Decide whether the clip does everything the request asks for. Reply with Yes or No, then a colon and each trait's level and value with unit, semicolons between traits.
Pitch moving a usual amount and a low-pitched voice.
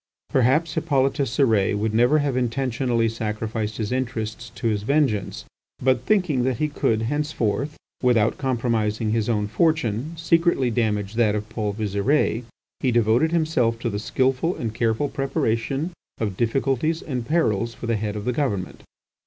Yes: average, 3.9 semitones; low, 120 Hz